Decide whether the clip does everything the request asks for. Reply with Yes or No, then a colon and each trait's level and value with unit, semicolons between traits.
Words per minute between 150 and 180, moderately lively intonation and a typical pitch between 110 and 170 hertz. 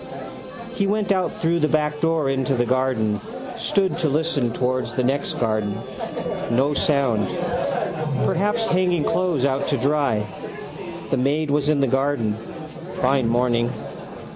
No: slow, 135 wpm; average, 4.3 semitones; medium, 140 Hz